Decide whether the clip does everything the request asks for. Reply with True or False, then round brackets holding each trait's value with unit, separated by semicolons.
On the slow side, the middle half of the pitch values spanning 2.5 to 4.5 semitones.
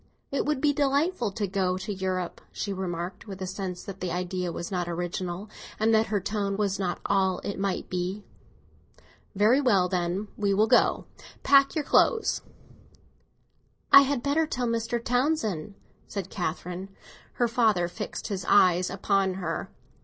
False (165 wpm; 4.1 semitones)